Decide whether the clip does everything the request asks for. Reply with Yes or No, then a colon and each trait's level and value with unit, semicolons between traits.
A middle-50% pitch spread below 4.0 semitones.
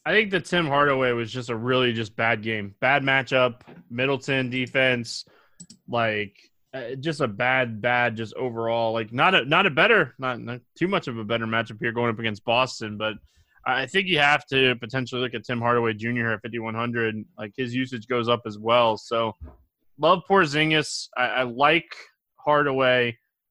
Yes: average, 2.7 semitones